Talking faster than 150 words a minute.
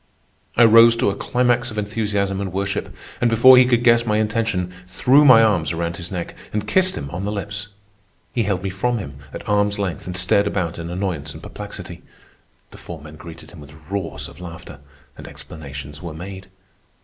Yes: average, 195 wpm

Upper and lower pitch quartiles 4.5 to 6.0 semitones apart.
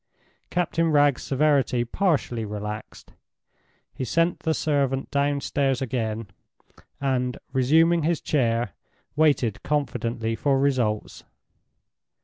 No: average, 4.1 semitones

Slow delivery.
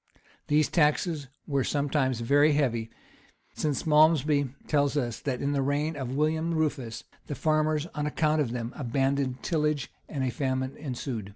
No: average, 155 wpm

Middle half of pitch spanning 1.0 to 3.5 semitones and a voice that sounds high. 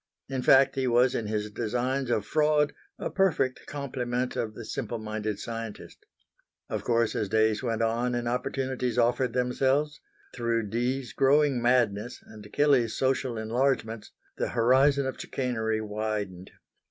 No: average, 3.1 semitones; low, 120 Hz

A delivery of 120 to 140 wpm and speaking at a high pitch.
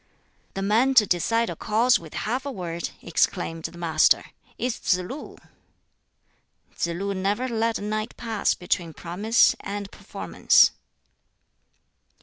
Yes: slow, 135 wpm; high, 205 Hz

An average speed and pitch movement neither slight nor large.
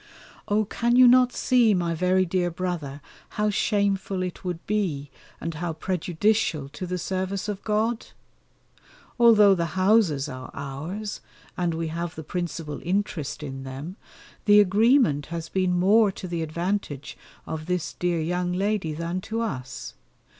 Yes: average, 150 wpm; average, 4.2 semitones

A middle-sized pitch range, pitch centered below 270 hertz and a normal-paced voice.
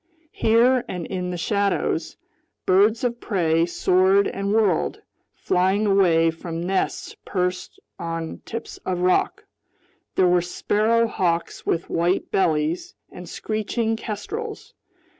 No: average, 3.7 semitones; medium, 185 Hz; slow, 120 wpm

